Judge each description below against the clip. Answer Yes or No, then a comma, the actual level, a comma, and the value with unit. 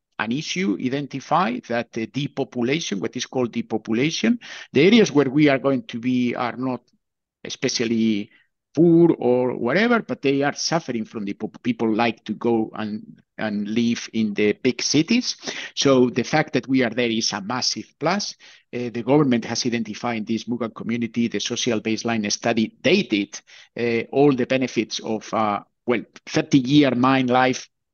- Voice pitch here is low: Yes, low, 120 Hz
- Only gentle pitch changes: No, average, 3.3 semitones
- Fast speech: No, average, 160 wpm